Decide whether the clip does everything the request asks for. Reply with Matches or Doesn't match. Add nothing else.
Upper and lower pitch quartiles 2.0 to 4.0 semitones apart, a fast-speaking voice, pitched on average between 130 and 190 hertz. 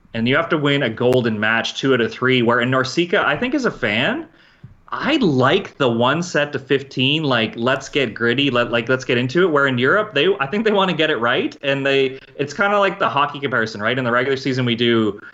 Matches